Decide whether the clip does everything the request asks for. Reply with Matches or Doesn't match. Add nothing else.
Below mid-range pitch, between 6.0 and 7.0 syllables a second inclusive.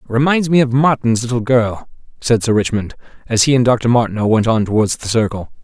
Doesn't match